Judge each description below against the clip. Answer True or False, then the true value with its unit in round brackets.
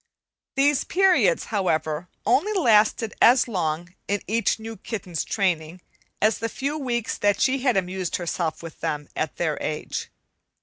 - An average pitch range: False (6.4 semitones)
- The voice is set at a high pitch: True (210 Hz)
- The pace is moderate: True (145 wpm)